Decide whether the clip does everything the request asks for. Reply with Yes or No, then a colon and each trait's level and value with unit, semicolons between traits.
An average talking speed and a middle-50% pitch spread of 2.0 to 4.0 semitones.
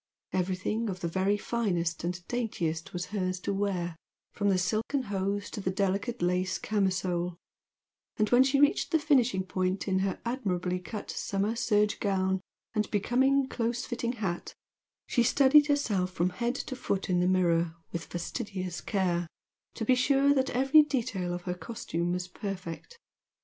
No: average, 160 wpm; average, 4.8 semitones